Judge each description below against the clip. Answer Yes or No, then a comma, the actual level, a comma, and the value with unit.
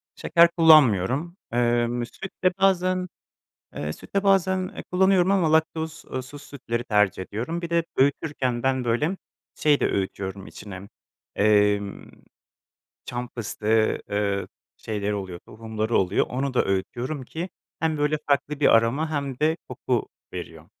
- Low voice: Yes, low, 130 Hz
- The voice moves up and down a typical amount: No, wide, 7.0 semitones